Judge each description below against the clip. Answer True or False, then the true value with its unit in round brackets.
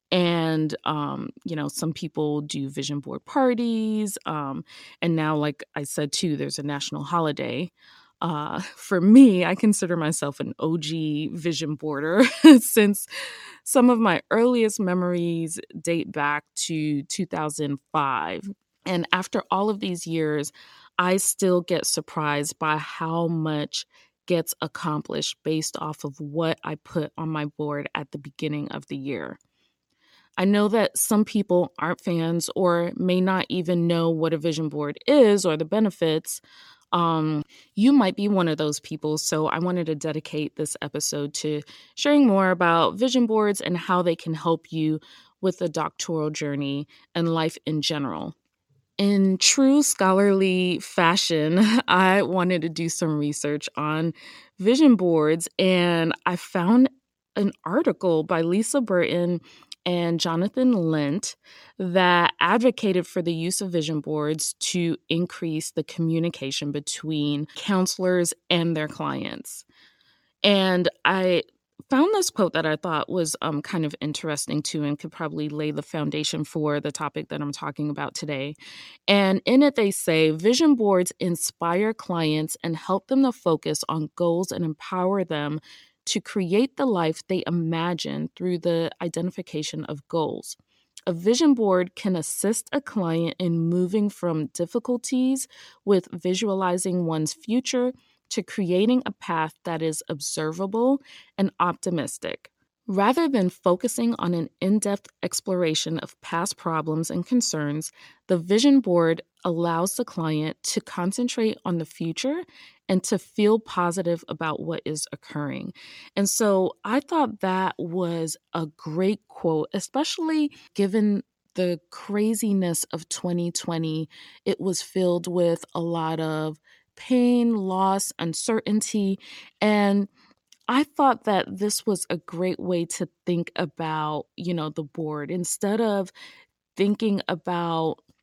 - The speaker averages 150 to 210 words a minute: False (140 wpm)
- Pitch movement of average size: True (4.2 semitones)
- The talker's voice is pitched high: False (175 Hz)